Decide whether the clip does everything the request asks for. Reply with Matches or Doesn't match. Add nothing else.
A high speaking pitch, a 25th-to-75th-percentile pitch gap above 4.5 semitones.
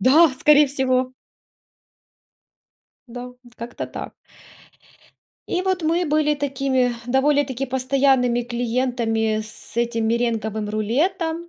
Doesn't match